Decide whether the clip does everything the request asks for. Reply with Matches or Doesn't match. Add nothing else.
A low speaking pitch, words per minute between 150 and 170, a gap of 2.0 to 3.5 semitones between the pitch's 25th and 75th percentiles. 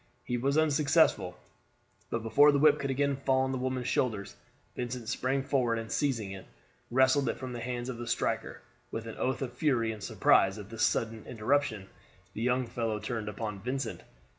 Doesn't match